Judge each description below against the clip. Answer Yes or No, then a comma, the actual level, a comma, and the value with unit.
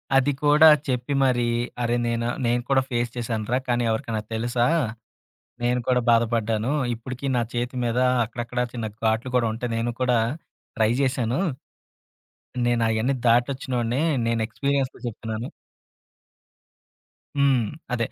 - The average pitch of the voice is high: No, low, 120 Hz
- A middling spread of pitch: No, narrow, 1.7 semitones